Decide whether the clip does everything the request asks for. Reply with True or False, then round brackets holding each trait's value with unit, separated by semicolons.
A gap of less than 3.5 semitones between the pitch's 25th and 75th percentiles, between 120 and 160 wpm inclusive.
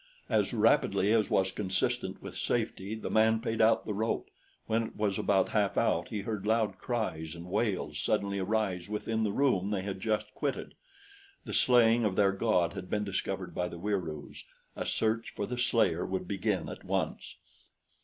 False (2.9 semitones; 180 wpm)